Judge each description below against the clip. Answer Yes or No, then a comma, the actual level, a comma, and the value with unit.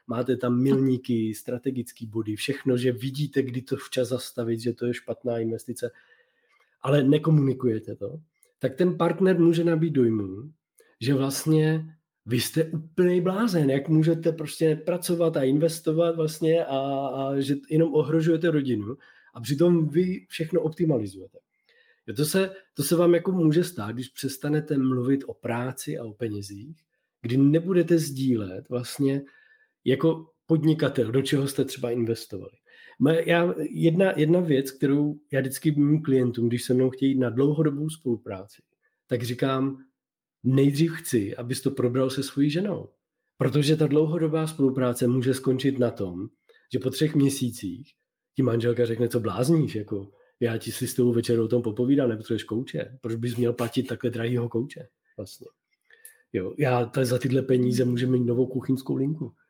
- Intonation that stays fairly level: No, average, 4.5 semitones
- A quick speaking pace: No, average, 150 wpm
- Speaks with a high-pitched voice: No, low, 135 Hz